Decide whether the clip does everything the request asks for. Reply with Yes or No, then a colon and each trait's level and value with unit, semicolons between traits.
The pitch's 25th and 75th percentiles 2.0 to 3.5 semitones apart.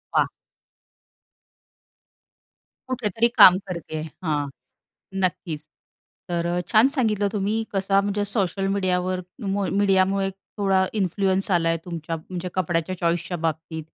Yes: average, 2.8 semitones